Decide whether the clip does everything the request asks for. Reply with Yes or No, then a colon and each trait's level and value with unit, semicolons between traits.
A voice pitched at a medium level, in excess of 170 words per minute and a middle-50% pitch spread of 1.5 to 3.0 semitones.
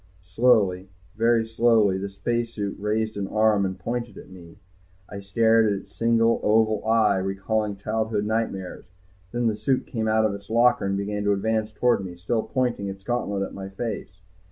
No: low, 110 Hz; average, 180 wpm; narrow, 2.6 semitones